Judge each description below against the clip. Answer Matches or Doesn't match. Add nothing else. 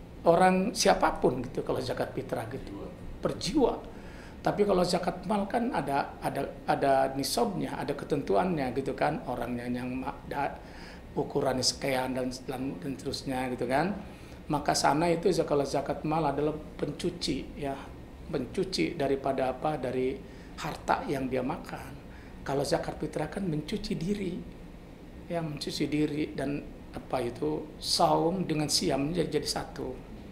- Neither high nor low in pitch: Matches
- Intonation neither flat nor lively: Matches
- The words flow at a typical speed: Matches